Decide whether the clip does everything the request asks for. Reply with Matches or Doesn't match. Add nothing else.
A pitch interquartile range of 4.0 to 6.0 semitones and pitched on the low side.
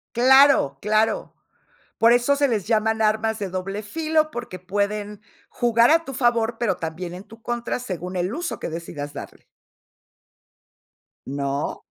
Doesn't match